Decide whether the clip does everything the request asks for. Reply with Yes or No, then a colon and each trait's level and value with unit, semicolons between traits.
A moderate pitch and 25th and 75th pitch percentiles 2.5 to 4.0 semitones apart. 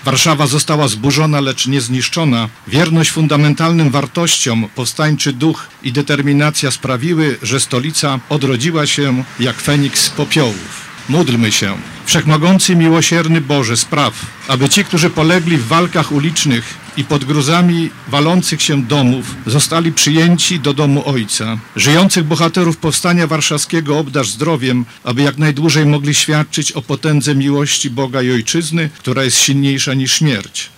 Yes: medium, 145 Hz; average, 3.3 semitones